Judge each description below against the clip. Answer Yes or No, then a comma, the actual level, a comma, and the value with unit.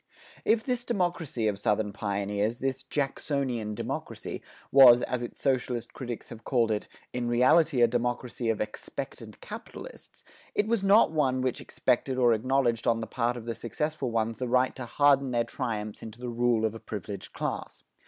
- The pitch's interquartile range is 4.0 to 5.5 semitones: No, average, 3.0 semitones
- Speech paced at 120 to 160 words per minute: No, average, 175 wpm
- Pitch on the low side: Yes, low, 120 Hz